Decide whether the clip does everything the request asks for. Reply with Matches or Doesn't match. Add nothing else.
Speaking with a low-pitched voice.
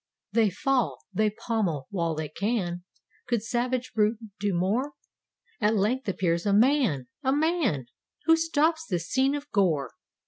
Doesn't match